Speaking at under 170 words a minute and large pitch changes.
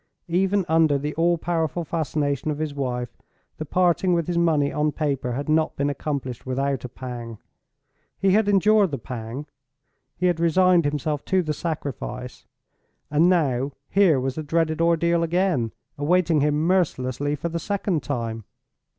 No: average, 160 wpm; average, 3.7 semitones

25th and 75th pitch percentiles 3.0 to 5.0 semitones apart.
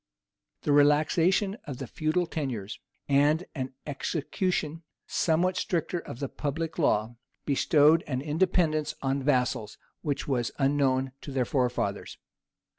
Yes: average, 3.4 semitones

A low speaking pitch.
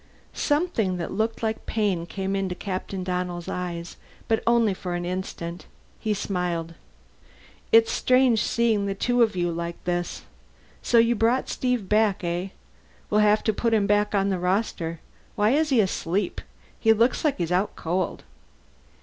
No: high, 200 Hz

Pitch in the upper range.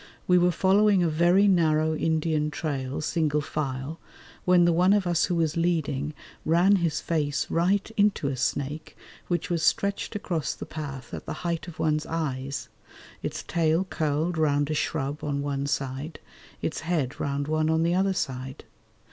No: medium, 160 Hz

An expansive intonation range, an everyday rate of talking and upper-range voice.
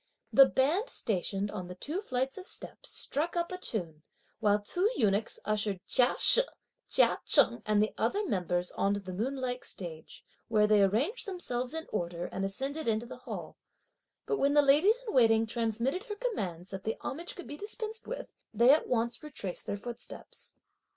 Yes: wide, 7.3 semitones; average, 180 wpm; high, 235 Hz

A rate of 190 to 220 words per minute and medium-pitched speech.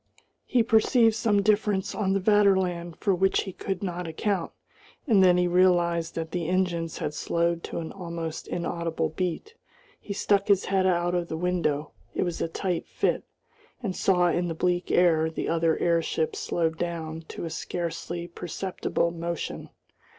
No: average, 165 wpm; medium, 175 Hz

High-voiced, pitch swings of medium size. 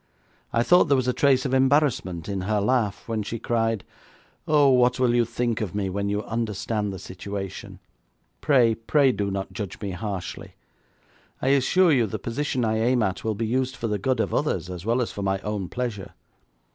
No: low, 115 Hz; average, 4.0 semitones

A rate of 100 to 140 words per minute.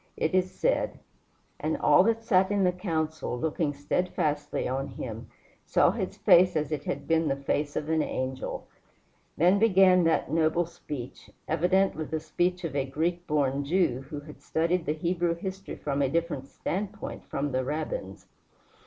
No: average, 165 wpm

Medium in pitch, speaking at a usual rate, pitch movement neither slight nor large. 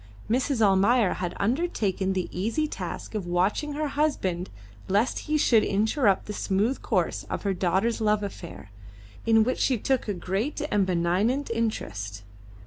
No: high, 210 Hz; average, 150 wpm; average, 4.7 semitones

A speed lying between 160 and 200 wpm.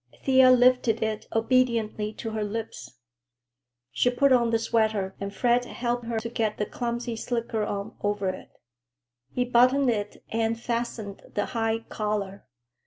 No: average, 150 wpm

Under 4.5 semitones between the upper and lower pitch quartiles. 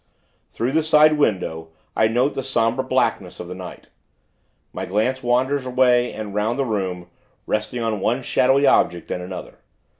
No: average, 4.8 semitones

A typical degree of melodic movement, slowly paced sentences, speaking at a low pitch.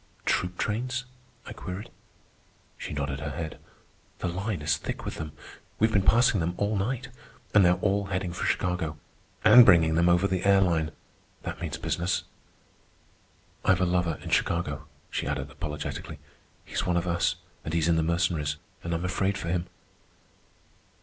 No: average, 3.1 semitones; average, 165 wpm; very low, 90 Hz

